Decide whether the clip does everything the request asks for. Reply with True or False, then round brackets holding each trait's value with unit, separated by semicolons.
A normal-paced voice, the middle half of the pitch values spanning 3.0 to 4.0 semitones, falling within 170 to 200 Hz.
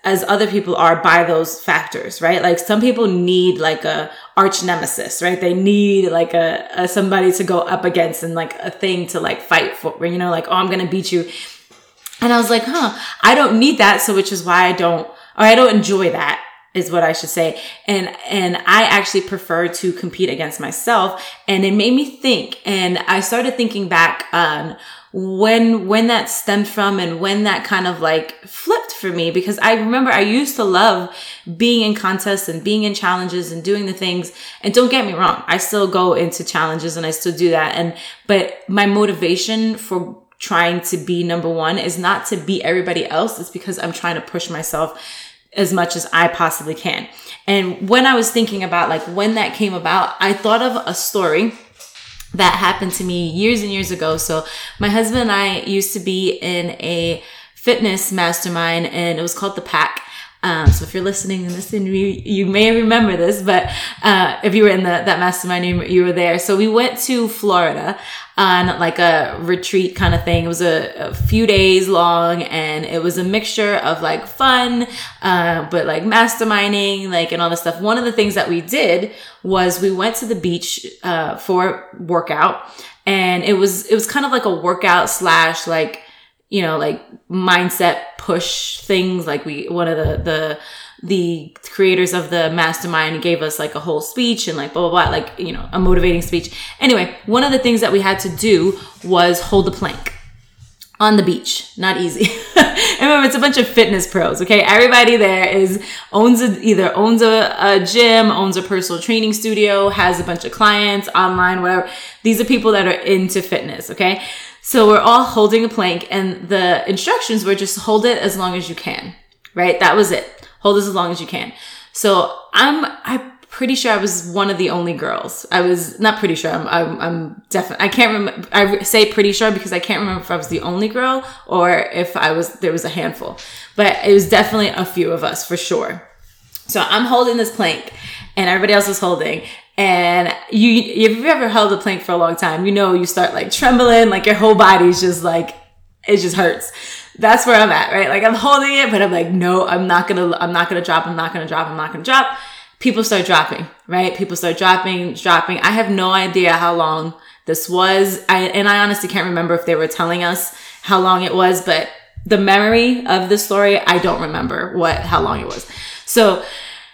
False (210 wpm; 3.6 semitones; 190 Hz)